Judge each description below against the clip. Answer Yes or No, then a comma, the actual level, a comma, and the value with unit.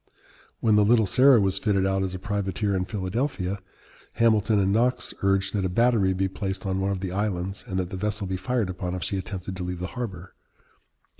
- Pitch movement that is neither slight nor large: No, narrow, 2.3 semitones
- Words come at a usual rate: No, fast, 215 wpm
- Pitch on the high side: No, very low, 95 Hz